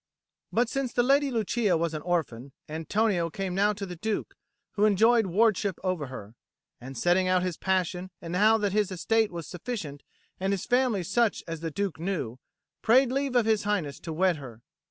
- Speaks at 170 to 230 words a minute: Yes, average, 195 wpm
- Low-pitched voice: No, high, 190 Hz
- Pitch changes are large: No, average, 4.8 semitones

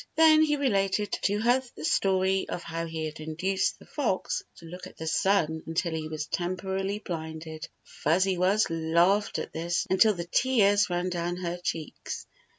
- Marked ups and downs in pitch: No, average, 3.4 semitones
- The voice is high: No, medium, 180 Hz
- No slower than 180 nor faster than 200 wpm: No, average, 170 wpm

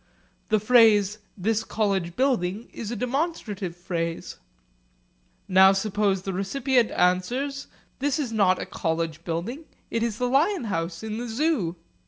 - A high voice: Yes, high, 215 Hz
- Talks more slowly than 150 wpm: Yes, average, 140 wpm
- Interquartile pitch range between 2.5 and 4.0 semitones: No, average, 5.2 semitones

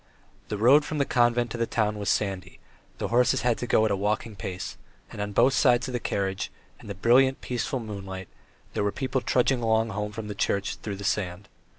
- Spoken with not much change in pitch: No, average, 3.3 semitones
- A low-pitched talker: Yes, low, 110 Hz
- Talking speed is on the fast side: Yes, fast, 215 wpm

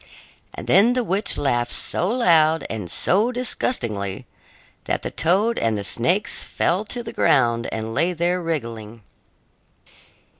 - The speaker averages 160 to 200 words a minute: No, average, 140 wpm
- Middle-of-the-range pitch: Yes, medium, 165 Hz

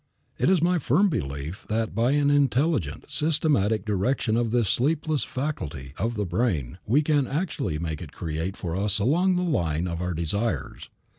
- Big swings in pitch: Yes, wide, 9.0 semitones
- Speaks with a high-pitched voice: No, low, 115 Hz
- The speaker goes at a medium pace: Yes, average, 170 wpm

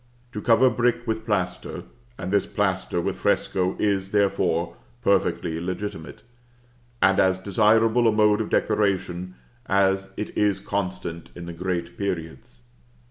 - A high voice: No, very low, 95 Hz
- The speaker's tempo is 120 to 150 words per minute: Yes, slow, 135 wpm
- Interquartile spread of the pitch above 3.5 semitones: No, average, 2.7 semitones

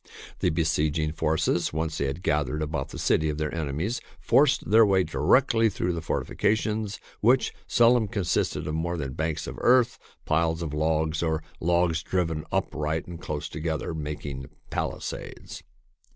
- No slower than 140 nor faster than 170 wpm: Yes, average, 150 wpm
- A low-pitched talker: Yes, very low, 80 Hz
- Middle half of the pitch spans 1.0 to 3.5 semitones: Yes, average, 3.2 semitones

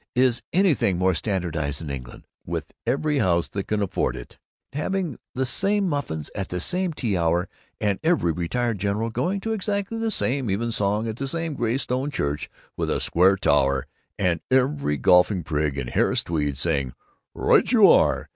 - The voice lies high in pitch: No, low, 105 Hz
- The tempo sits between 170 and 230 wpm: Yes, average, 175 wpm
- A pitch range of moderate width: No, wide, 9.0 semitones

